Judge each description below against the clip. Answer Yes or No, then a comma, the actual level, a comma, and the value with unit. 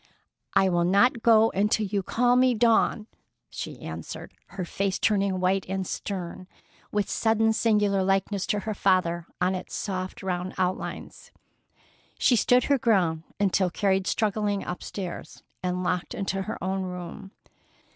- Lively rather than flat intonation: No, narrow, 2.5 semitones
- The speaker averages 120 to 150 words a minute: Yes, average, 145 wpm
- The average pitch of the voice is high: Yes, high, 195 Hz